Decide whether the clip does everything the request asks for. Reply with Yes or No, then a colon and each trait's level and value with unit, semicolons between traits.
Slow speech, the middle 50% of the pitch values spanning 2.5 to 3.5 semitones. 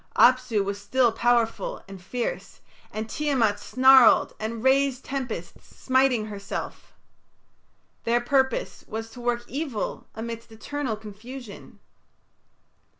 Yes: slow, 105 wpm; average, 3.2 semitones